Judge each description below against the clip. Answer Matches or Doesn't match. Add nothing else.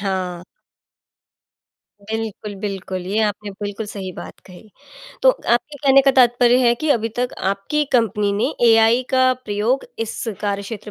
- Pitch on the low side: Doesn't match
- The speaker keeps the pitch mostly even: Doesn't match